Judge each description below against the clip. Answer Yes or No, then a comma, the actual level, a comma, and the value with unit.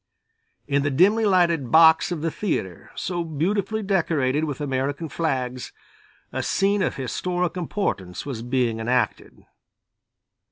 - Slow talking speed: Yes, slow, 125 wpm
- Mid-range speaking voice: Yes, medium, 155 Hz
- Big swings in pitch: Yes, wide, 5.7 semitones